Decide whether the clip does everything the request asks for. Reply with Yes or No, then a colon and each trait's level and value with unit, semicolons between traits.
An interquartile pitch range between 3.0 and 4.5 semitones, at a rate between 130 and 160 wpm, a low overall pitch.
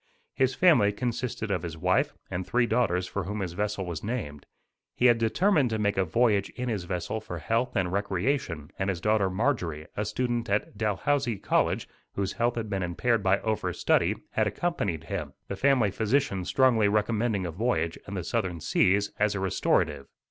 No: average, 4.2 semitones; average, 185 wpm; low, 105 Hz